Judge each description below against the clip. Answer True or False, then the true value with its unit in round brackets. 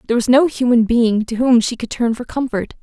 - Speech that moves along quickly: True (255 wpm)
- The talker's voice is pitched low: False (240 Hz)